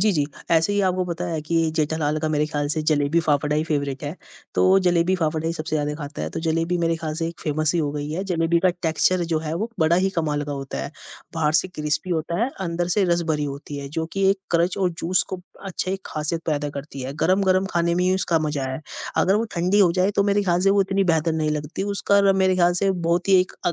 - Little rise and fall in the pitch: No, average, 3.4 semitones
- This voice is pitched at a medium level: Yes, medium, 165 Hz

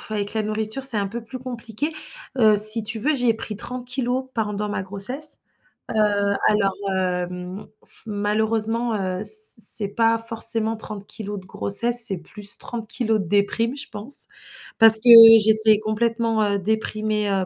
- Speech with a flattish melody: Yes, narrow, 2.0 semitones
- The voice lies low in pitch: No, high, 215 Hz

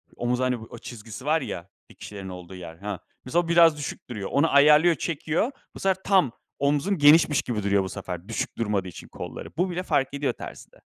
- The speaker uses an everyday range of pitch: No, wide, 7.8 semitones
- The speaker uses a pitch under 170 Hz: Yes, low, 135 Hz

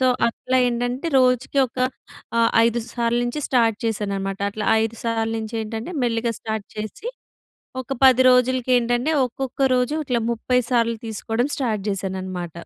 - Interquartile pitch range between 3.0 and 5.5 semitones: No, narrow, 2.4 semitones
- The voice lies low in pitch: No, high, 235 Hz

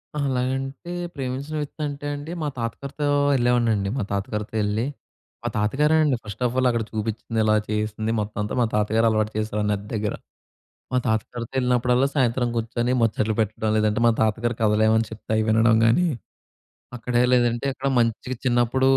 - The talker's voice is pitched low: Yes, low, 115 Hz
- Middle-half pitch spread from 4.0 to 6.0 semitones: No, average, 2.9 semitones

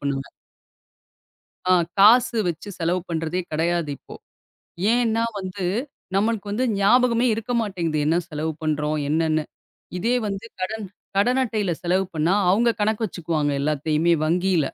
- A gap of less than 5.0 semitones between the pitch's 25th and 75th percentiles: No, wide, 5.4 semitones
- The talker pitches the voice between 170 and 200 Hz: Yes, medium, 185 Hz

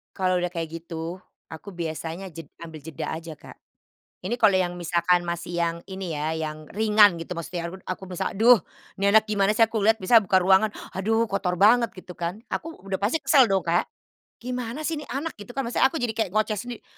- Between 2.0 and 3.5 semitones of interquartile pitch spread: No, average, 4.6 semitones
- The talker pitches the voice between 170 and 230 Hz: Yes, high, 190 Hz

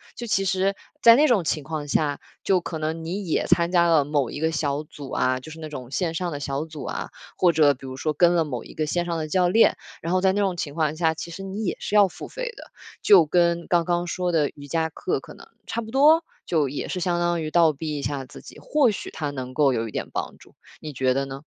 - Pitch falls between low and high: Yes, medium, 160 Hz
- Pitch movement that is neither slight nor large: Yes, average, 3.6 semitones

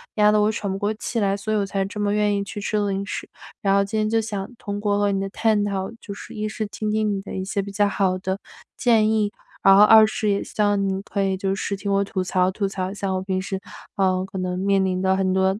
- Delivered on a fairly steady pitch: Yes, narrow, 1.6 semitones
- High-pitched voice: Yes, high, 200 Hz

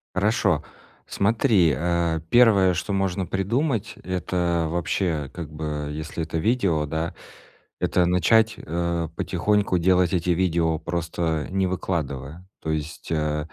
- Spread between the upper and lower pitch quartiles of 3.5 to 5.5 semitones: No, average, 3.0 semitones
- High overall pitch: No, very low, 85 Hz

